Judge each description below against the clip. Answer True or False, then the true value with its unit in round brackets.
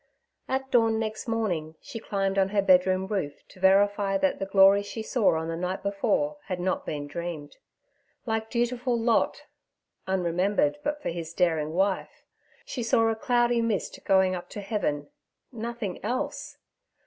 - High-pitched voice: True (195 Hz)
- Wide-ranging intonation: False (4.0 semitones)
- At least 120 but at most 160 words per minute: True (155 wpm)